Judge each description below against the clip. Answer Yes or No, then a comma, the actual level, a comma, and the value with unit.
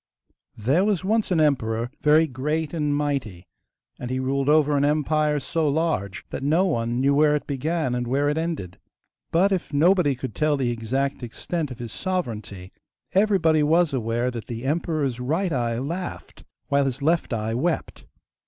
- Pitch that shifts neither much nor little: Yes, average, 4.6 semitones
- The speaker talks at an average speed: Yes, average, 170 wpm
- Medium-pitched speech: Yes, medium, 145 Hz